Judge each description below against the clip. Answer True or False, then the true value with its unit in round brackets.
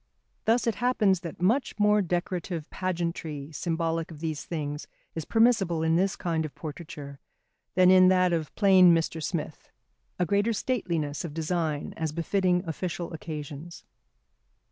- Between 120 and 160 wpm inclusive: True (145 wpm)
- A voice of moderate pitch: True (170 Hz)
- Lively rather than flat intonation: False (2.9 semitones)